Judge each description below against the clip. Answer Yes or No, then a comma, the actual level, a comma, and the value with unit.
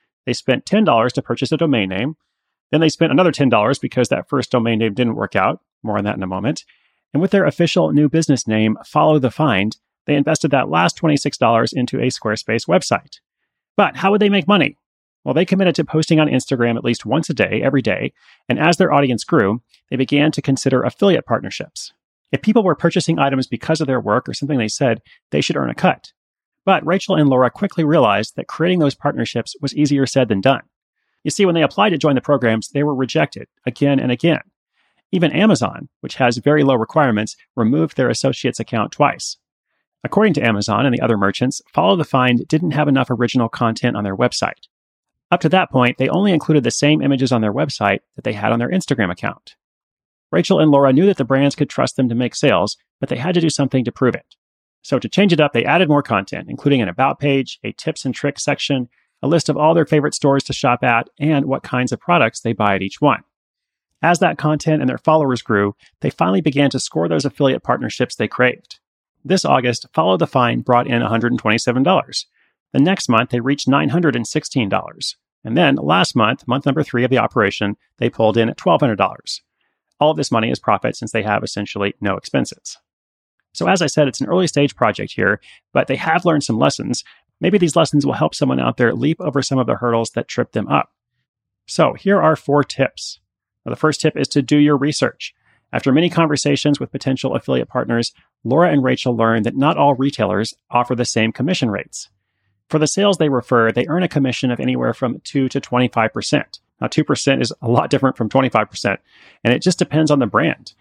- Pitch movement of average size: Yes, average, 4.5 semitones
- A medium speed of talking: No, fast, 215 wpm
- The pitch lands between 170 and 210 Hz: No, low, 135 Hz